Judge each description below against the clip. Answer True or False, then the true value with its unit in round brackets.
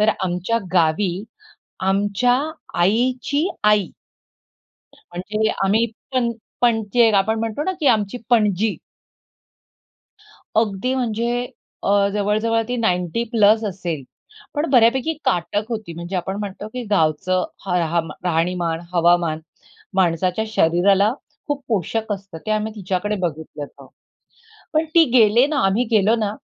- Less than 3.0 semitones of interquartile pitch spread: False (4.0 semitones)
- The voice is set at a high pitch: True (205 Hz)